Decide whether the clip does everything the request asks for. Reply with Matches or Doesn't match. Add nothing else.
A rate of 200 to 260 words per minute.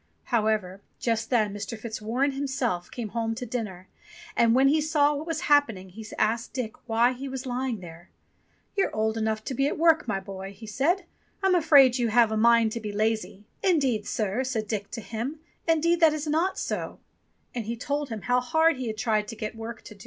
Matches